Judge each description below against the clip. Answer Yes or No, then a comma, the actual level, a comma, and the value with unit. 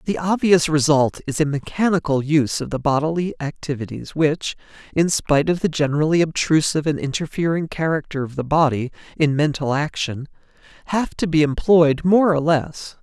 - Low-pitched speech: No, medium, 155 Hz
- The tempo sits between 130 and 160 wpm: Yes, average, 155 wpm